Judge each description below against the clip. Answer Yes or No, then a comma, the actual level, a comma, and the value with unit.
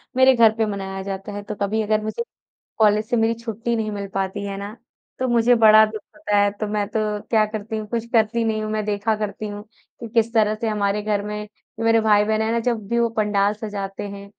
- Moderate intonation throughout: No, narrow, 1.6 semitones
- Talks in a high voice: Yes, high, 215 Hz